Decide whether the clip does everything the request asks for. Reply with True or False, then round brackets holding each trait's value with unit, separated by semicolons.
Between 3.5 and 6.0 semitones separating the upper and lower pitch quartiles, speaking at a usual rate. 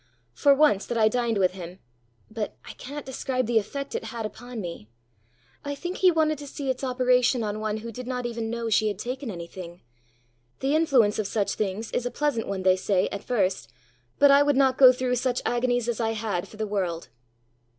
False (4.0 semitones; 215 wpm)